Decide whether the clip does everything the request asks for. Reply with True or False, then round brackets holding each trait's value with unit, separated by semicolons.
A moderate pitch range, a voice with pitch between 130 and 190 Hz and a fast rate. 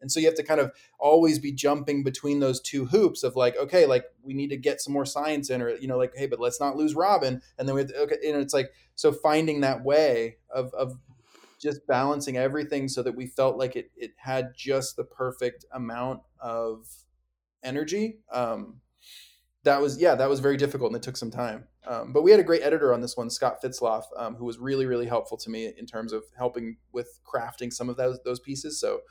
True (3.4 semitones; 135 Hz; 235 wpm)